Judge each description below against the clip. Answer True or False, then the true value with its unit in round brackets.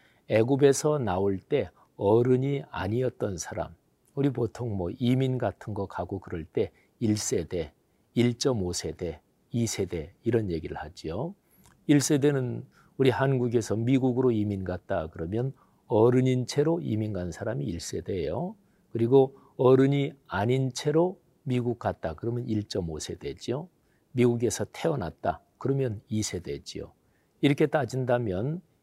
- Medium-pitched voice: False (120 Hz)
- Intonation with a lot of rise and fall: False (4.5 semitones)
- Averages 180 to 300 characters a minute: True (250 characters per minute)